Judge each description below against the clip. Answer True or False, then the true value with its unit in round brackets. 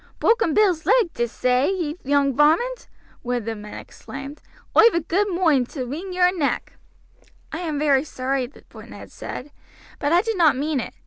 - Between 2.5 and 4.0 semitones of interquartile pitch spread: False (5.2 semitones)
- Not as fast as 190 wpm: True (180 wpm)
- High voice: True (300 Hz)